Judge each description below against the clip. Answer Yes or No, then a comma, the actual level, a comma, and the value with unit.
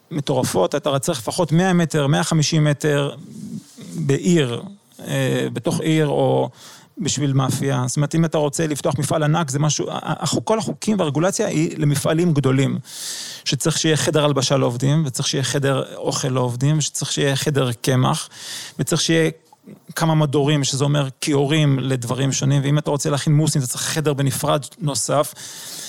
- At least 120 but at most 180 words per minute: Yes, fast, 150 wpm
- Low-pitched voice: No, medium, 150 Hz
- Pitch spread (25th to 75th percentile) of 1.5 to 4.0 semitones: Yes, average, 2.7 semitones